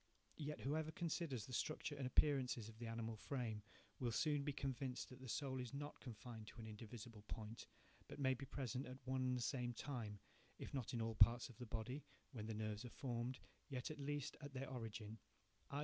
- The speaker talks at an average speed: No, fast, 210 wpm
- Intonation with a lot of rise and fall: No, average, 3.5 semitones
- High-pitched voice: No, low, 125 Hz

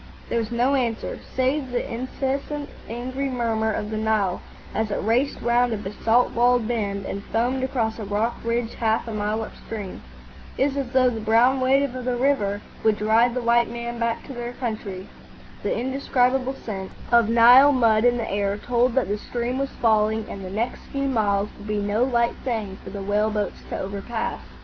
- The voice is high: Yes, high, 235 Hz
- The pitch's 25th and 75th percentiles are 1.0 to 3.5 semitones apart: Yes, average, 2.8 semitones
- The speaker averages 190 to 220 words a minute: Yes, average, 195 wpm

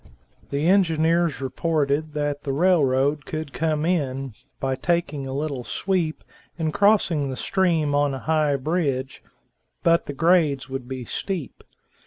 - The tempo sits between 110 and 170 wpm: Yes, average, 140 wpm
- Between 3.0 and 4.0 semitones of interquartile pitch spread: Yes, average, 3.5 semitones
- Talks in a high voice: No, medium, 150 Hz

